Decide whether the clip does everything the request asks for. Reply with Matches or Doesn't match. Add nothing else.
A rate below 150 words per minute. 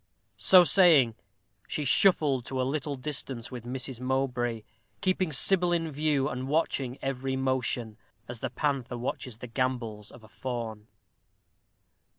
Matches